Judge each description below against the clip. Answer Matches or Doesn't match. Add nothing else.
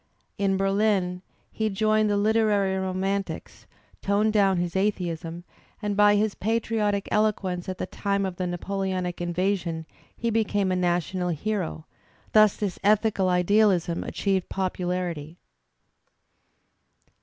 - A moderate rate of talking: Doesn't match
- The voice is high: Matches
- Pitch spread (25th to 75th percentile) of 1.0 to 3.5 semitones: Matches